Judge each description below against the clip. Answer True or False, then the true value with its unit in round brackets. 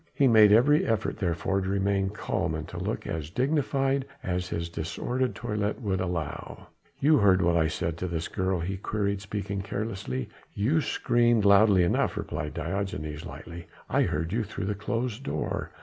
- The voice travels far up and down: False (4.4 semitones)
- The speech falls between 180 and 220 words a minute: False (170 wpm)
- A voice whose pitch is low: True (100 Hz)